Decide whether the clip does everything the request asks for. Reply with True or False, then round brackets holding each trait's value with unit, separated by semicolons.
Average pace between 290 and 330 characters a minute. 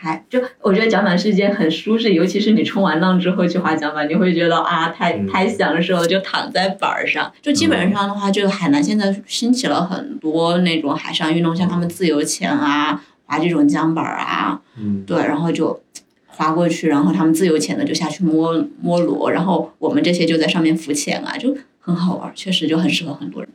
True (320 characters per minute)